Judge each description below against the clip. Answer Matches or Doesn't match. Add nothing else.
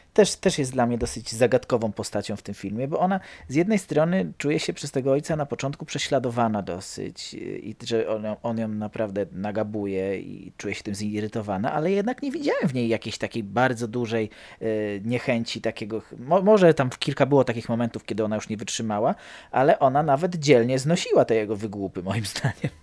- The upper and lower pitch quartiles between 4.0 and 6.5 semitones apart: Matches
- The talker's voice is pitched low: Matches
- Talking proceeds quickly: Matches